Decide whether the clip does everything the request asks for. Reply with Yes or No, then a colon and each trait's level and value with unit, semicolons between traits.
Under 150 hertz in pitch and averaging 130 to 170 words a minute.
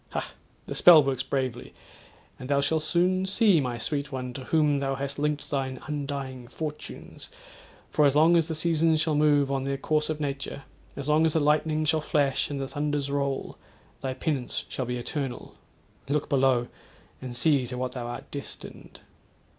No: medium, 140 Hz; average, 180 wpm